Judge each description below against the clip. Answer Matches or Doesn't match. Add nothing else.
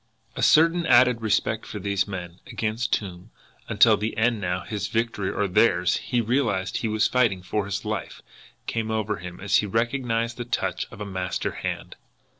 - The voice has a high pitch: Doesn't match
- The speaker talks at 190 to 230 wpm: Doesn't match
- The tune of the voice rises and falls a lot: Doesn't match